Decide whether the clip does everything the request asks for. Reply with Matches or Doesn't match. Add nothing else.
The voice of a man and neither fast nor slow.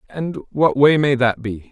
Doesn't match